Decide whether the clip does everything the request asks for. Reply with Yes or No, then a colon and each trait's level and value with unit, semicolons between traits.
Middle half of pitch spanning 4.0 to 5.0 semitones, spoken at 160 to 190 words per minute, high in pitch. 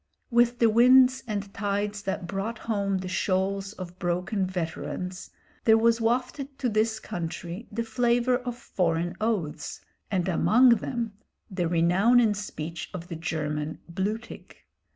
No: average, 4.4 semitones; average, 140 wpm; high, 200 Hz